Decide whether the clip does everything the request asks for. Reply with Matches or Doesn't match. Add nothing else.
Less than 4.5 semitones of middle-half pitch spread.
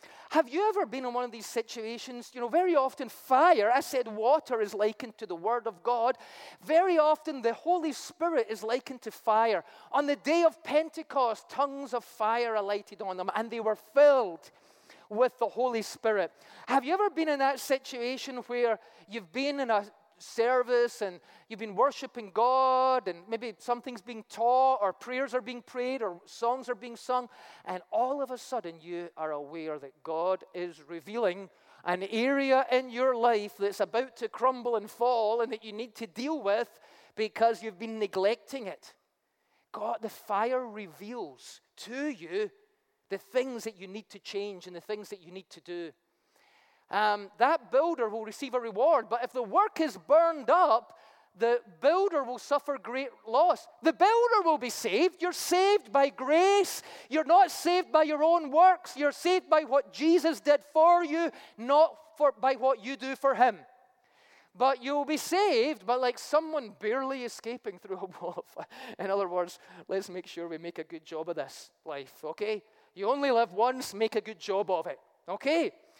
Doesn't match